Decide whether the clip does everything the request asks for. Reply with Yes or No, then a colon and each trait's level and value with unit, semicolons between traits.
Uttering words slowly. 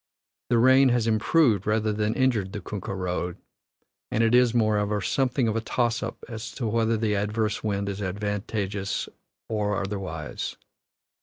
No: average, 155 wpm